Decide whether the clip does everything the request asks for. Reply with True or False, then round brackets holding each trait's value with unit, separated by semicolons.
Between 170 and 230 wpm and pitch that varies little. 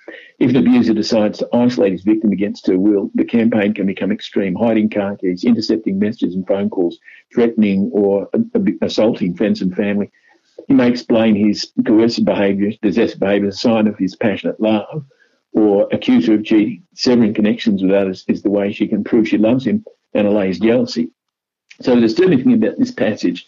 False (185 wpm; 3.6 semitones)